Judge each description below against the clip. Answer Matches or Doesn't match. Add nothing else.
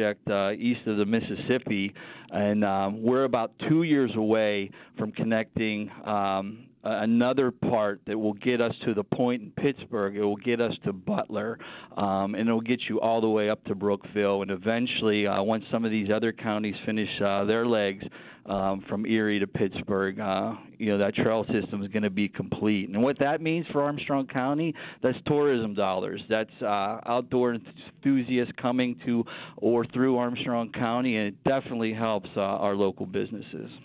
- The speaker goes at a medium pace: Matches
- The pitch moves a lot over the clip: Doesn't match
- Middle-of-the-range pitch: Doesn't match